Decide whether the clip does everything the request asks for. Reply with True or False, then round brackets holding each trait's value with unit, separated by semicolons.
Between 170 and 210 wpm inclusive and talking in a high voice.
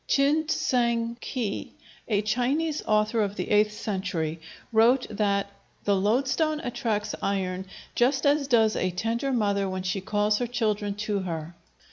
False (145 wpm; 215 Hz)